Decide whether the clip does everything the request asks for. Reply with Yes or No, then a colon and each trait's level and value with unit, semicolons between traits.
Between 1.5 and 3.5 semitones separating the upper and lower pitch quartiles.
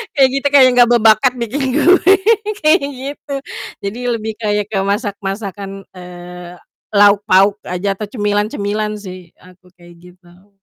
No: average, 4.1 semitones